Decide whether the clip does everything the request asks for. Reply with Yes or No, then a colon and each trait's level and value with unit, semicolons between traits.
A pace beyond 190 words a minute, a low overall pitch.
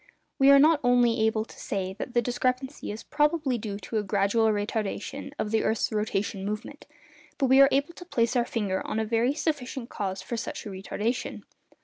No: average, 200 wpm; high, 230 Hz